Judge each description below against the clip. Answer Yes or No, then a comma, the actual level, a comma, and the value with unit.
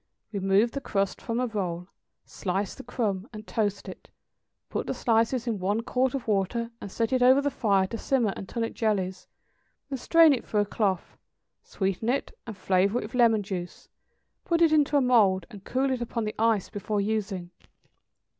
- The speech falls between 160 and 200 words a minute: Yes, average, 190 wpm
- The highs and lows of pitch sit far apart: No, average, 3.8 semitones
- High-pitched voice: Yes, high, 220 Hz